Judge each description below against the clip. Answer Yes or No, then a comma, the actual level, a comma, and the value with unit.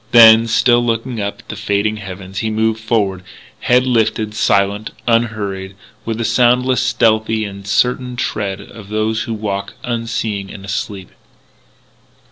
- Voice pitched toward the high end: No, low, 110 Hz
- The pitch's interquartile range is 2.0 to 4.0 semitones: Yes, narrow, 2.4 semitones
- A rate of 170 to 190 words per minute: No, average, 140 wpm